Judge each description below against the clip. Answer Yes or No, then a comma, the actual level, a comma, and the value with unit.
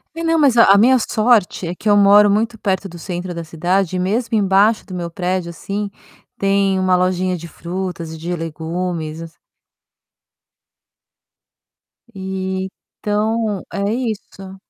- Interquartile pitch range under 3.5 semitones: Yes, average, 2.8 semitones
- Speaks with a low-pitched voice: No, high, 190 Hz